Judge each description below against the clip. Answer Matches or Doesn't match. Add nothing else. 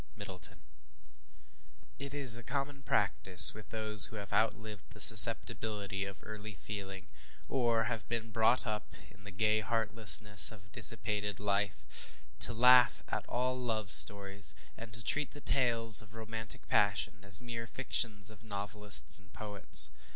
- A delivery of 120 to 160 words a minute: Matches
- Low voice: Matches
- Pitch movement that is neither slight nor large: Doesn't match